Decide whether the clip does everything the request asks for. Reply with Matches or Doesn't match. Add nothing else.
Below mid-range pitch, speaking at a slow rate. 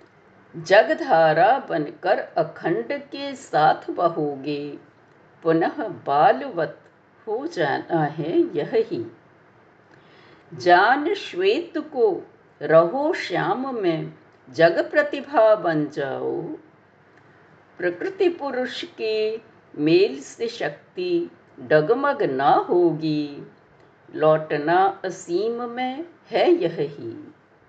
Doesn't match